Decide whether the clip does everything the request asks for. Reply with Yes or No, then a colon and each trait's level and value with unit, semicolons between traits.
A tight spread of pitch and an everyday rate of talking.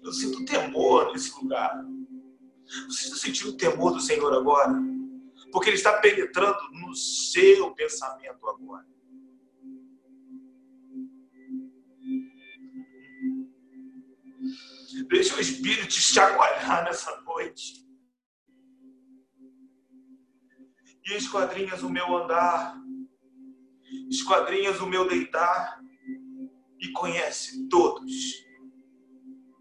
No: narrow, 2.0 semitones; slow, 80 wpm